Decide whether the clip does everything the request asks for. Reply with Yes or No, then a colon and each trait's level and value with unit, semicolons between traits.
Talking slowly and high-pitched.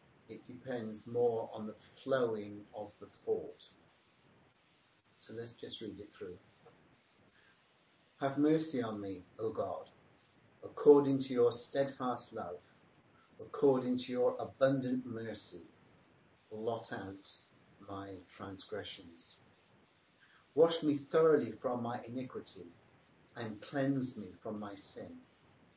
No: slow, 110 wpm; low, 120 Hz